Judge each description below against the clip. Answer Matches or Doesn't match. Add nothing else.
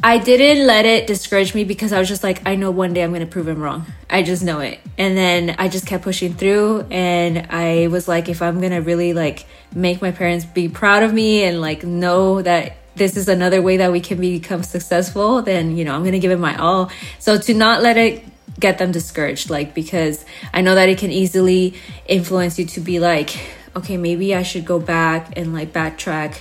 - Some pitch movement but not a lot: Doesn't match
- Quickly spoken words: Matches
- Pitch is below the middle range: Doesn't match